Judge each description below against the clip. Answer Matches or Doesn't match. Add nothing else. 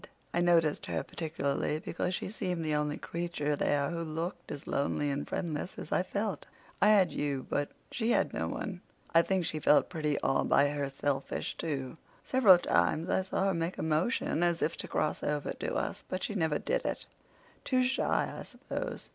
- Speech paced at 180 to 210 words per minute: Matches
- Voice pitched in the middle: Matches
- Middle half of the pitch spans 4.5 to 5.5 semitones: Doesn't match